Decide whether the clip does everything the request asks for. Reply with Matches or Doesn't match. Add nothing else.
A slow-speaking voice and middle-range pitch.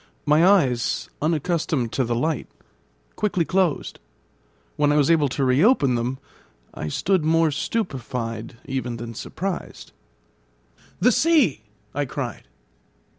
Matches